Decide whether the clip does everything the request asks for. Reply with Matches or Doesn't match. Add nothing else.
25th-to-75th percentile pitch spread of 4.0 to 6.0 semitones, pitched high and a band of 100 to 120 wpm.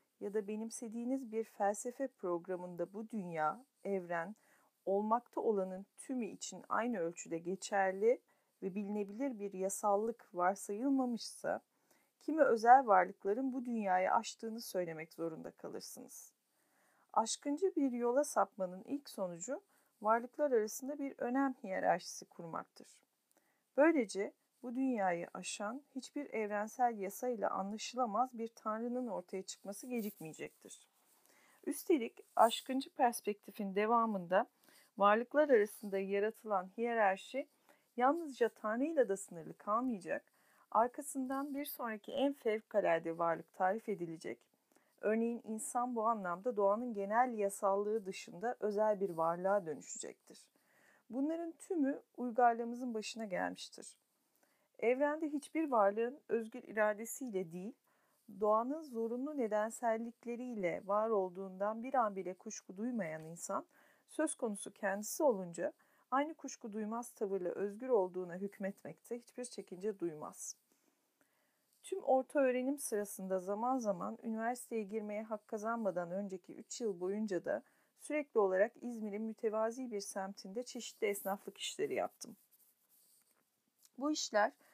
Matches